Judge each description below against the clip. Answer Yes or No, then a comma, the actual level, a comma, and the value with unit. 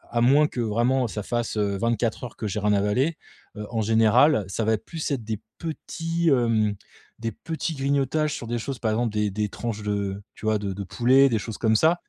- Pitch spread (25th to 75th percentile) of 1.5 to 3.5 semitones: No, average, 4.2 semitones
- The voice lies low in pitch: Yes, low, 115 Hz